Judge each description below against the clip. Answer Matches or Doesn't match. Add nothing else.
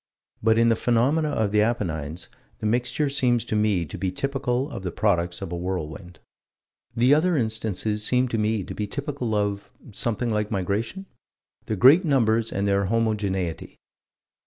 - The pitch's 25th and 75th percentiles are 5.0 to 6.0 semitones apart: Doesn't match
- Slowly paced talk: Doesn't match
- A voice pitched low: Matches